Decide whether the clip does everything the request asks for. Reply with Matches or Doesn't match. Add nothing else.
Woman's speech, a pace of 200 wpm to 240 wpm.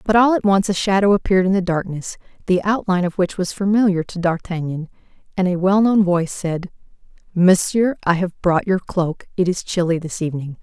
Doesn't match